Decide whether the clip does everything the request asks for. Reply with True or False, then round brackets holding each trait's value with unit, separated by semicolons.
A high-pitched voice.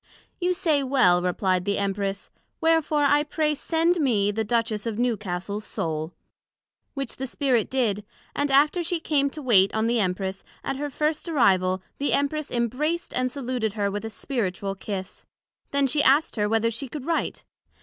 True (245 Hz)